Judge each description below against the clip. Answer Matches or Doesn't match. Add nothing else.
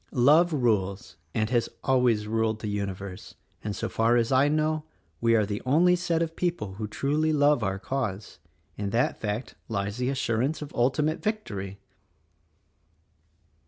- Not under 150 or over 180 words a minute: Matches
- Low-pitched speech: Matches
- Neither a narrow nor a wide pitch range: Doesn't match